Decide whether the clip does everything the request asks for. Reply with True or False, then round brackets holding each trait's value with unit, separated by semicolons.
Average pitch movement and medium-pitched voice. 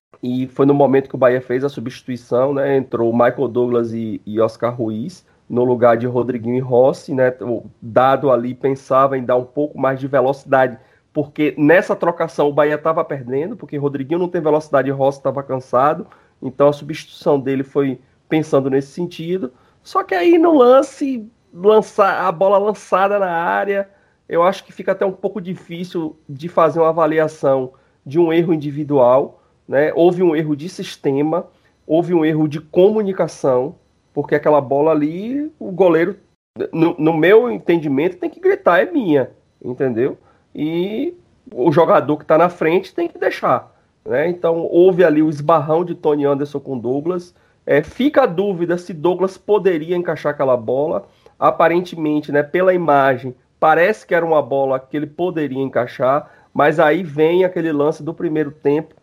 True (4.6 semitones; 155 Hz)